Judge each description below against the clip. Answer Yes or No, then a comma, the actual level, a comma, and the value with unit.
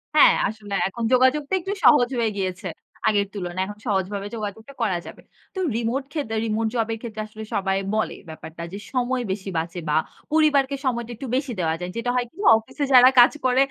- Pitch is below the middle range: No, high, 225 Hz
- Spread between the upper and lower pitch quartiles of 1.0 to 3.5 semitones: No, average, 4.4 semitones